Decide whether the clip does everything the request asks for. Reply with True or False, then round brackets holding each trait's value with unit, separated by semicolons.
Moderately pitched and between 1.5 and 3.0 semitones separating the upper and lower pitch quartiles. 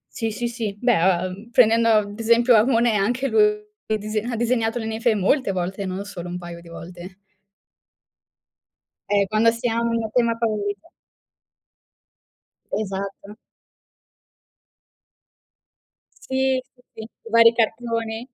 False (220 Hz; 2.7 semitones)